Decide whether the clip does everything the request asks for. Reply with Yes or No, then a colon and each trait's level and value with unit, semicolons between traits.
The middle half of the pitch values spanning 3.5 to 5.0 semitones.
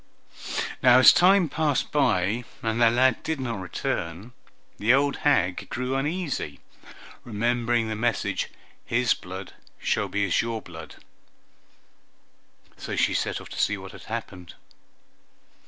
Yes: average, 4.3 semitones